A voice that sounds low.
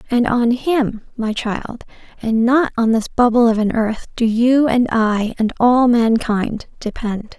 No: high, 230 Hz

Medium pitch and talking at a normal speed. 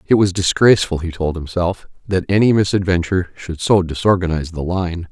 No: very low, 90 Hz; average, 165 wpm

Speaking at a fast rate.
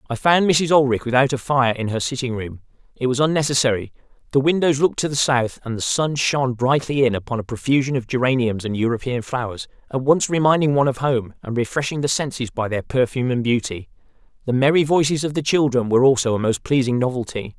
Yes: fast, 210 wpm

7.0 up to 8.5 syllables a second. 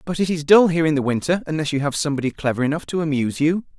Yes: 7.6 syllables/s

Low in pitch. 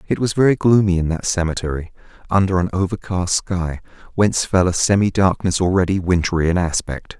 Yes: very low, 90 Hz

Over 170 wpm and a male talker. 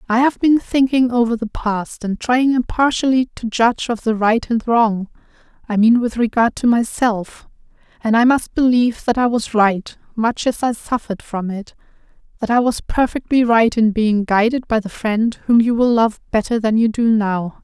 No: average, 195 wpm; female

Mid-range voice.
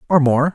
Yes: medium, 150 Hz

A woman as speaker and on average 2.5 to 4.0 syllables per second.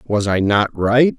No: male; 3.5 syllables/s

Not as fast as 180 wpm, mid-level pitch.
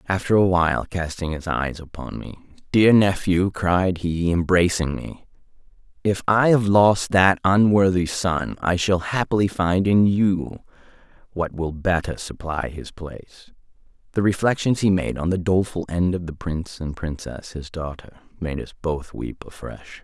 No: average, 160 wpm; very low, 90 Hz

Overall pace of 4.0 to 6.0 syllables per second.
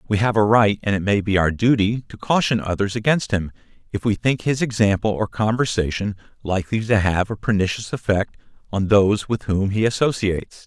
Yes: 5.5 syllables/s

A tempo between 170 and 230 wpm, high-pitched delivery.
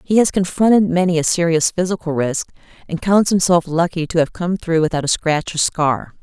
No: average, 200 wpm; medium, 170 Hz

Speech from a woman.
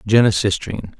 No: male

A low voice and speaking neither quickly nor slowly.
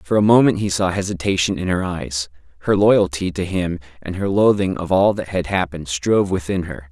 No: very low, 90 Hz; fast, 210 wpm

